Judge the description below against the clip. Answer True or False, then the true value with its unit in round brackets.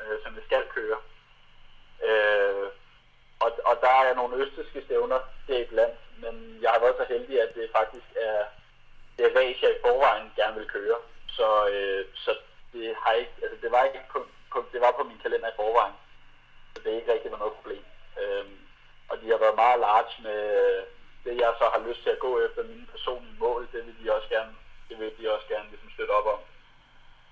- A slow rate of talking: False (210 wpm)